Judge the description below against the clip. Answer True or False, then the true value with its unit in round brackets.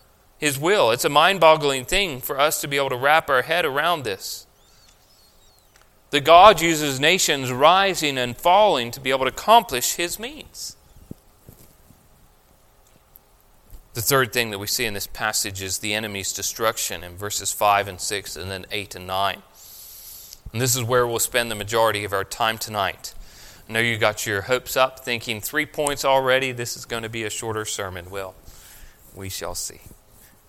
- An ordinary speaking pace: True (175 wpm)